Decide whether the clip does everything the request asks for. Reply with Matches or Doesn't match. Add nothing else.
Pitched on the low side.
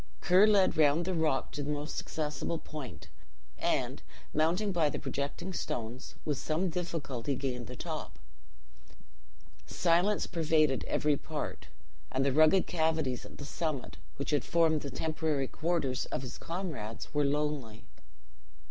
Doesn't match